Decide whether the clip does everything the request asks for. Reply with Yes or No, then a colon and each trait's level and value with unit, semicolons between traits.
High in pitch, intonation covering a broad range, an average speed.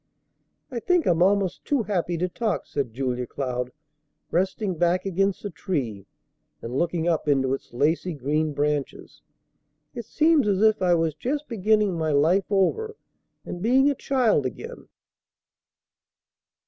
No: medium, 175 Hz; wide, 6.5 semitones; average, 145 wpm